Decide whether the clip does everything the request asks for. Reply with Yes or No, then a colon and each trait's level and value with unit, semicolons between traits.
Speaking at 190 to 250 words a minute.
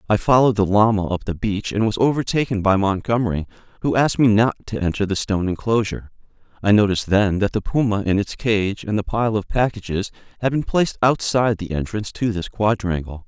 Yes: average, 200 wpm